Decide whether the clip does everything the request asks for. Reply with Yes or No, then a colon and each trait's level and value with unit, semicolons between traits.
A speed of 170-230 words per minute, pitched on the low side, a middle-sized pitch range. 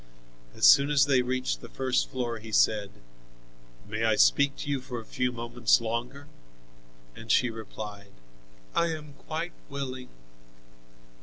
No: average, 145 wpm; low, 125 Hz; average, 3.7 semitones